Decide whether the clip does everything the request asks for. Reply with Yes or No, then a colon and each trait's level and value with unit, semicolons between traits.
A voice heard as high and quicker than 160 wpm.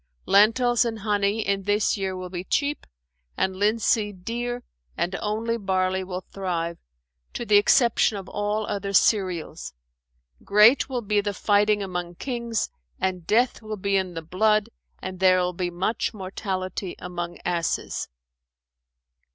No: high, 200 Hz; average, 145 wpm